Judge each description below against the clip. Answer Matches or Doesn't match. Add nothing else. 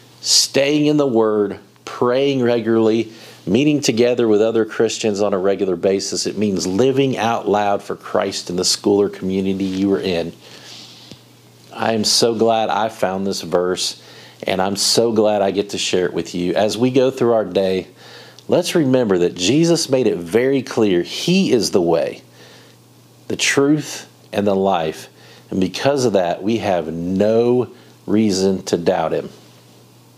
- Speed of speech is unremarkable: Matches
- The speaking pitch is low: Matches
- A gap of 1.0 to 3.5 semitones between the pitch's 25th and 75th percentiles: Doesn't match